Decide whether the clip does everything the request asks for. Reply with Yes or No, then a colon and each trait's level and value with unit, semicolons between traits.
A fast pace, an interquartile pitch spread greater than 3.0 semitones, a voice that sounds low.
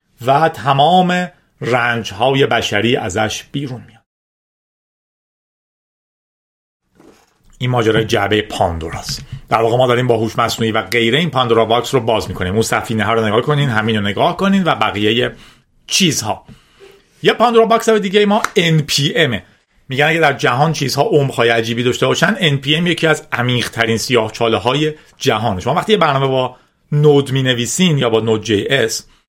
Yes: fast, 160 wpm; average, 5.2 semitones; low, 125 Hz